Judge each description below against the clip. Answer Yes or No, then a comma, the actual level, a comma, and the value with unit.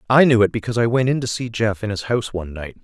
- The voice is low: Yes, low, 110 Hz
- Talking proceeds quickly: Yes, fast, 320 wpm